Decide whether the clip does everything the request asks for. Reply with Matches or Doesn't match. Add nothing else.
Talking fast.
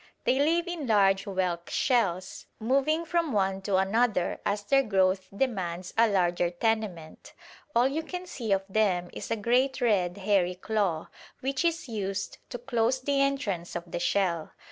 Doesn't match